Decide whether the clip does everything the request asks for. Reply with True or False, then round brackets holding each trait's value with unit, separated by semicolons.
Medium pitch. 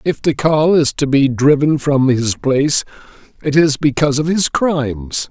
True (145 Hz)